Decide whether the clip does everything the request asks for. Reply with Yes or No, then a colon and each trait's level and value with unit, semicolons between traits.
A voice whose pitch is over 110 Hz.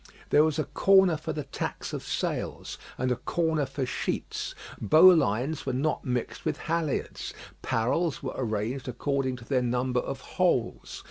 Yes: low, 135 Hz